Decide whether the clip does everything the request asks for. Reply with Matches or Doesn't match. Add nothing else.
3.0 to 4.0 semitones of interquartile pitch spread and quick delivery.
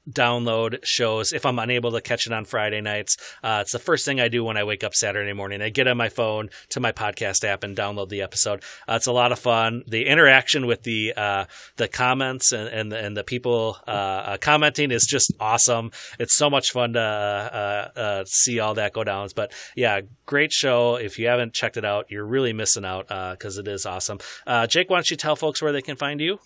Matches